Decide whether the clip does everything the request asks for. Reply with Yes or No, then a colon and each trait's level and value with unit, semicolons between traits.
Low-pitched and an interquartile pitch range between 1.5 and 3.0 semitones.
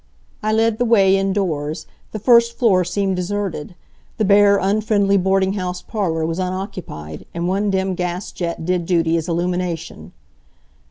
No: high, 190 Hz; average, 2.7 semitones